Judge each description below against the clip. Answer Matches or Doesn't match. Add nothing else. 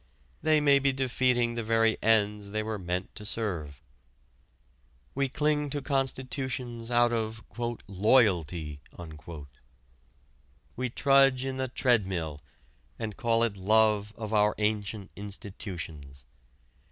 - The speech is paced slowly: Matches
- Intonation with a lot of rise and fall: Doesn't match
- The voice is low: Matches